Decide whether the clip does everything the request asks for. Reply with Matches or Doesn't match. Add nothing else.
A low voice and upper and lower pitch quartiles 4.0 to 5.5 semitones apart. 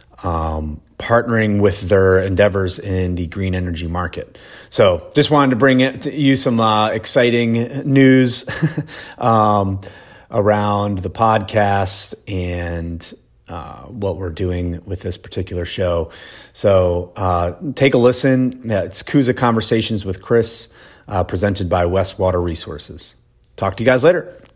Matches